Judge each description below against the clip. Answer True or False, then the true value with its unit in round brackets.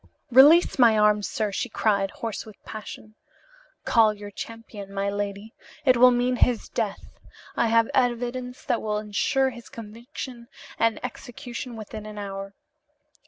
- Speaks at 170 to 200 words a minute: False (145 wpm)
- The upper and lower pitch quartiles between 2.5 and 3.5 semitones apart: True (2.8 semitones)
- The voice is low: False (225 Hz)